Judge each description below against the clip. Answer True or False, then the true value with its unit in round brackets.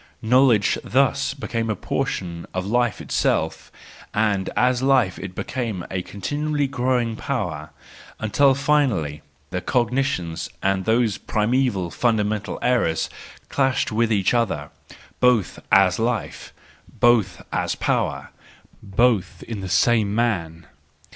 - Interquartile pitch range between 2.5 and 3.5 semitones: False (4.9 semitones)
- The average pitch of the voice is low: True (110 Hz)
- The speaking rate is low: True (115 wpm)